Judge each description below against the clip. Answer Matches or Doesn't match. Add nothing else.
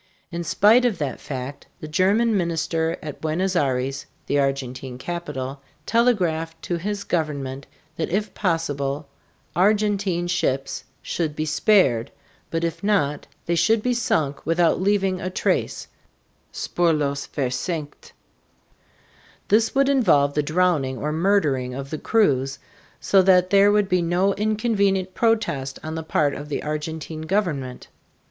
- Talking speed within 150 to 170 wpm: Doesn't match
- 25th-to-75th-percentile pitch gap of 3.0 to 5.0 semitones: Doesn't match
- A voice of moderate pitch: Matches